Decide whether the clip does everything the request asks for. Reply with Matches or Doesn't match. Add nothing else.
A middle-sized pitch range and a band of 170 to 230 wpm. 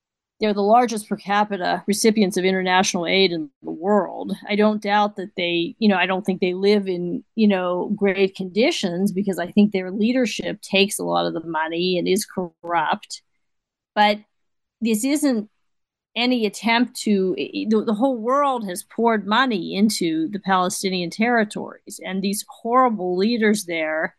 Doesn't match